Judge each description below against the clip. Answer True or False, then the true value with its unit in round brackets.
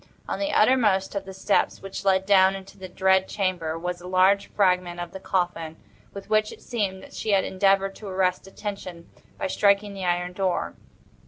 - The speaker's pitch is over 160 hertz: True (190 Hz)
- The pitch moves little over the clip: True (1.5 semitones)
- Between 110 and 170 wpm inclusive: False (190 wpm)